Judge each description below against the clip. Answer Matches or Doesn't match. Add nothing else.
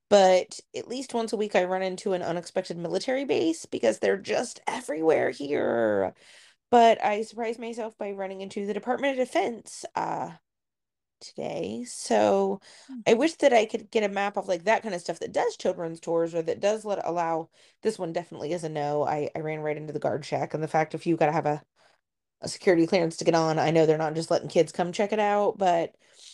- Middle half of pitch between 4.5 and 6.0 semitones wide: Matches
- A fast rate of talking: Matches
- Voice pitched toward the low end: Doesn't match